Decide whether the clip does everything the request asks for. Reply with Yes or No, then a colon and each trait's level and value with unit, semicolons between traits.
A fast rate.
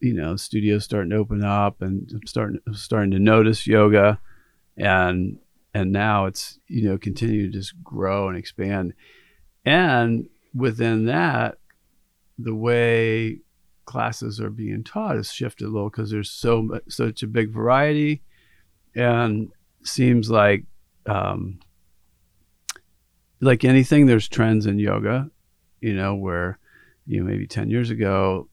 No: average, 140 wpm